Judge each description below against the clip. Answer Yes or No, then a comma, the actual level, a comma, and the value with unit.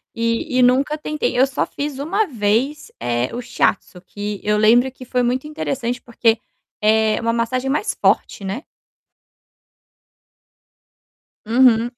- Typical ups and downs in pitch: Yes, average, 3.3 semitones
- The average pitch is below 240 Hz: No, high, 245 Hz